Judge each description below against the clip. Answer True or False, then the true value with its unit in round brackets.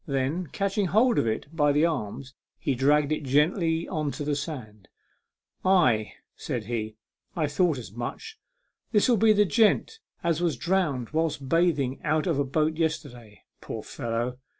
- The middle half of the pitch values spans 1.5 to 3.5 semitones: False (5.0 semitones)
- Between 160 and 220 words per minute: True (170 wpm)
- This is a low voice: False (150 Hz)